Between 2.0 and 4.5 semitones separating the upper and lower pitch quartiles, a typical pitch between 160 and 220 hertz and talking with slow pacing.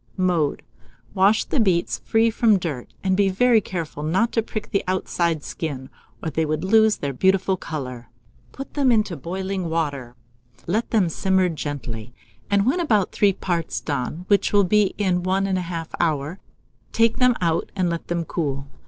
No: average, 4.2 semitones; medium, 185 Hz; average, 170 wpm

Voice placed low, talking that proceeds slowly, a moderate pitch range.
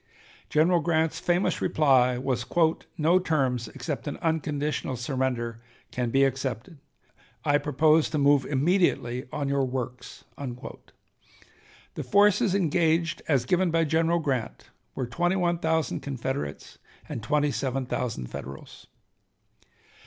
No: medium, 145 Hz; slow, 120 wpm; average, 4.3 semitones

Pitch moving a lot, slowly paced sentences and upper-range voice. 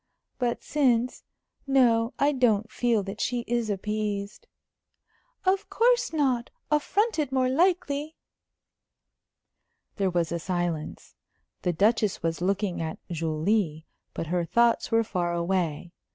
Yes: wide, 6.6 semitones; slow, 120 wpm; high, 220 Hz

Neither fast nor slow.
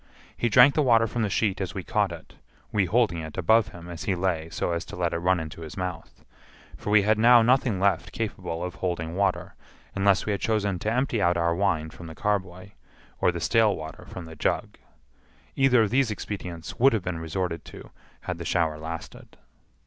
No: fast, 210 wpm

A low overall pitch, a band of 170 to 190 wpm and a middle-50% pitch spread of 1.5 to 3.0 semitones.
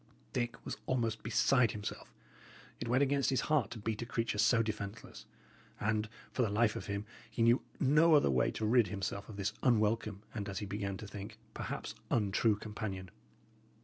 Yes: low, 110 Hz; average, 180 wpm; narrow, 2.6 semitones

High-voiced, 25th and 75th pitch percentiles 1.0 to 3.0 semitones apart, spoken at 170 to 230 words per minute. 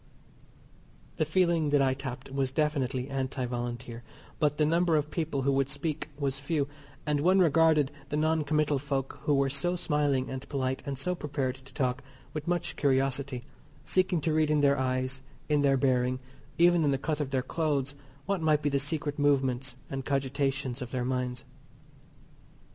No: medium, 140 Hz; narrow, 2.6 semitones; average, 175 wpm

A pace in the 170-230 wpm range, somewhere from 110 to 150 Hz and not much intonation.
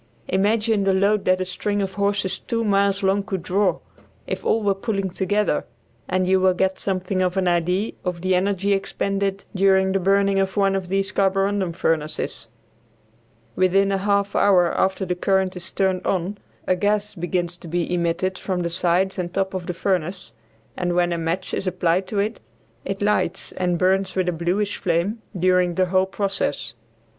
No: average, 185 wpm; high, 190 Hz; narrow, 1.7 semitones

